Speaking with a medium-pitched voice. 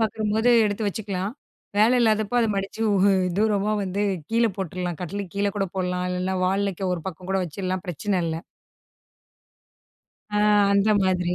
No: high, 195 Hz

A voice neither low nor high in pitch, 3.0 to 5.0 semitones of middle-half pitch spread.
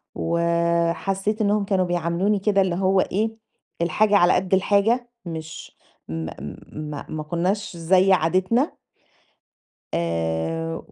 Yes: medium, 180 Hz; average, 3.4 semitones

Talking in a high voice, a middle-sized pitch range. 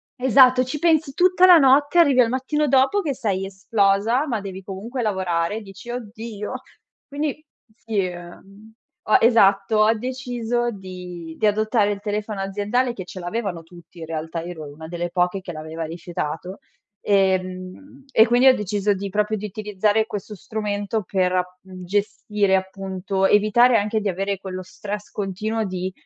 Yes: high, 205 Hz; average, 4.0 semitones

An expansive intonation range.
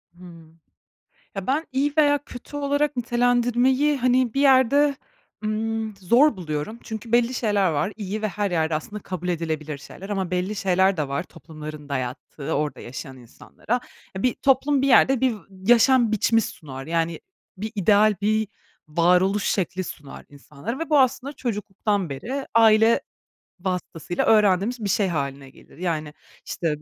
Yes: wide, 6.5 semitones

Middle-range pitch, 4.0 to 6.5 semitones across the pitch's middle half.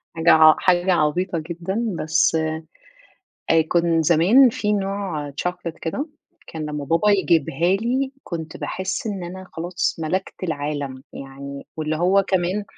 No: medium, 170 Hz; average, 3.5 semitones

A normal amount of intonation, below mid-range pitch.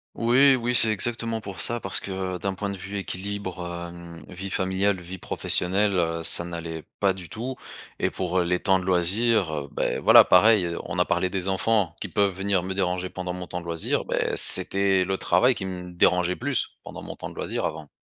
No: narrow, 2.3 semitones; very low, 95 Hz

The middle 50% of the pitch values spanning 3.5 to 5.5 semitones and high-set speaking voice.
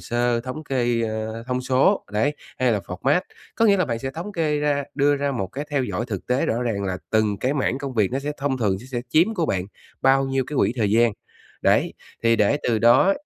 No: average, 4.0 semitones; low, 125 Hz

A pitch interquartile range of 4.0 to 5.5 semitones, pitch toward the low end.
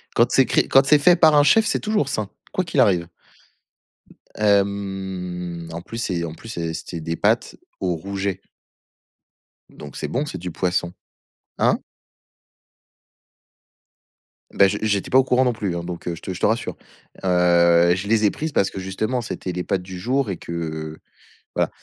Yes: average, 4.7 semitones; very low, 95 Hz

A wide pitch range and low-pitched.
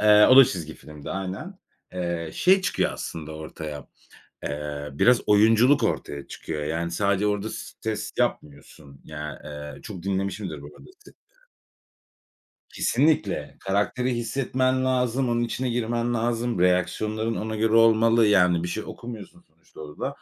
Yes: wide, 6.3 semitones; low, 105 Hz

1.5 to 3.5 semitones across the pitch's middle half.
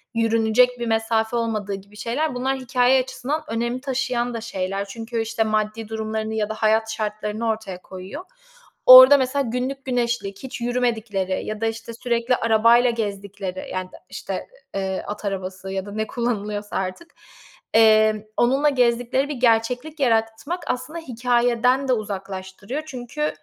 Yes: average, 2.9 semitones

